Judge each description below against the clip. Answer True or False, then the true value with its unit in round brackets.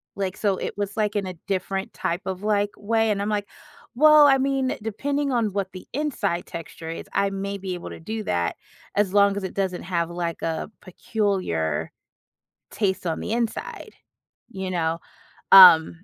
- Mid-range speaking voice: False (195 Hz)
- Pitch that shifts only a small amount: False (3.1 semitones)